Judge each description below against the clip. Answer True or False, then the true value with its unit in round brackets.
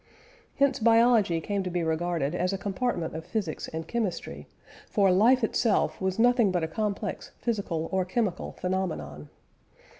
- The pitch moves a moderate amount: True (4.7 semitones)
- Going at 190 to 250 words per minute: False (150 wpm)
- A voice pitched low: False (190 Hz)